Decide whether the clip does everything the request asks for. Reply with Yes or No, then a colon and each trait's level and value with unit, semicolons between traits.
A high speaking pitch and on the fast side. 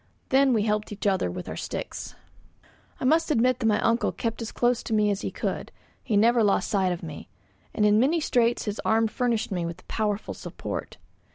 Yes: high, 220 Hz; fast, 210 wpm